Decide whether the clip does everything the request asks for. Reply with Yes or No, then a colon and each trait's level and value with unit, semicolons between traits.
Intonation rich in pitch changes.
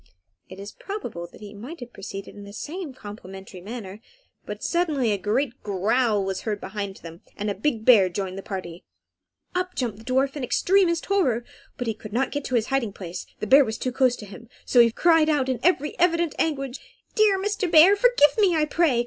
Yes: wide, 7.3 semitones